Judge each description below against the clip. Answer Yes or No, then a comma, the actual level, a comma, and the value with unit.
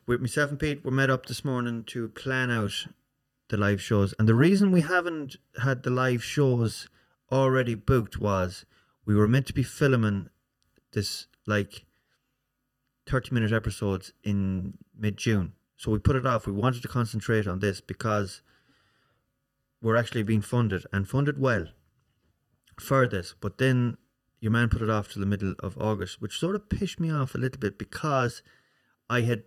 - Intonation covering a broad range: No, average, 4.1 semitones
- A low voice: Yes, low, 120 Hz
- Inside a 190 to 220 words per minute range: No, average, 175 wpm